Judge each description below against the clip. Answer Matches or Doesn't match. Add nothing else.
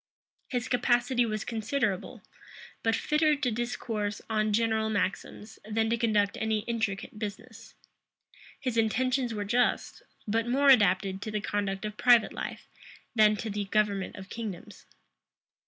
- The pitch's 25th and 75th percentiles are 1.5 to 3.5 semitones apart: Matches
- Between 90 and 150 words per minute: Matches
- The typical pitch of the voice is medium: Doesn't match